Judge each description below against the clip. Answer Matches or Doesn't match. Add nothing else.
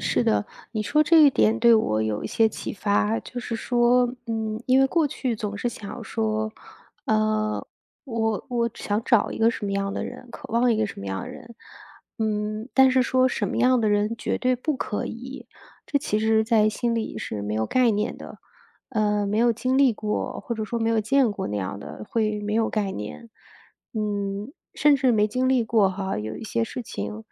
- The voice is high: Matches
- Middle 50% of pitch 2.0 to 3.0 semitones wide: Matches